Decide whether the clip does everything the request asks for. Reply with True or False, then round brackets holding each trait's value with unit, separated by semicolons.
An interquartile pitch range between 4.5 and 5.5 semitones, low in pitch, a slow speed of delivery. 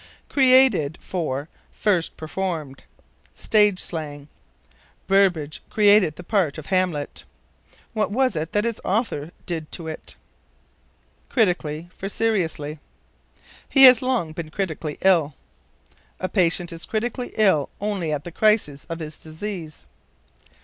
False (5.1 semitones; 175 Hz; 120 wpm)